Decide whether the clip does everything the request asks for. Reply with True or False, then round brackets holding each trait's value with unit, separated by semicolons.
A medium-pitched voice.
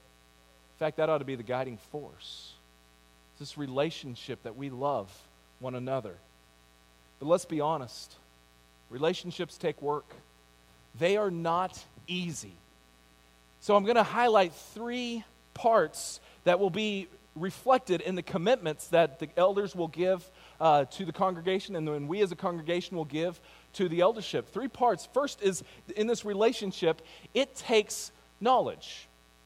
True (155 Hz)